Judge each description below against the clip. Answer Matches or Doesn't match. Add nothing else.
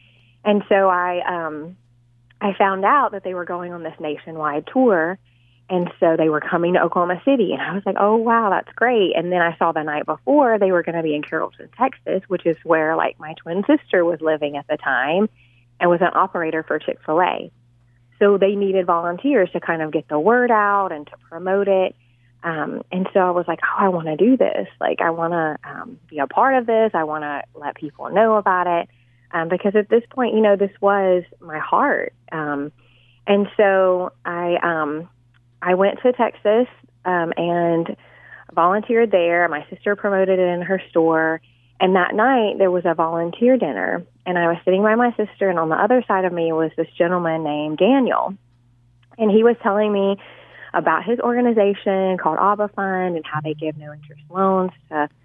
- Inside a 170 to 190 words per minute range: Doesn't match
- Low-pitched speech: Doesn't match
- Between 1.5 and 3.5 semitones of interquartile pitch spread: Doesn't match